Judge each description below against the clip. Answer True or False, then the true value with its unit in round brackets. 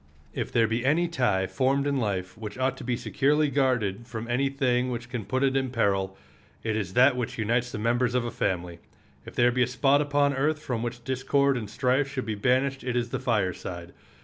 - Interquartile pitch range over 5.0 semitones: False (3.4 semitones)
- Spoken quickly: True (220 wpm)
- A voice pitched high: False (125 Hz)